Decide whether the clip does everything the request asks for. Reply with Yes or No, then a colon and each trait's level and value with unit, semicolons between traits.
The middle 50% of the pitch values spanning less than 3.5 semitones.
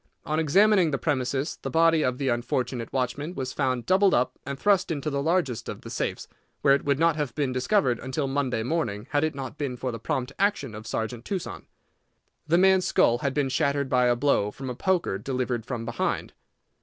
No: average, 4.0 semitones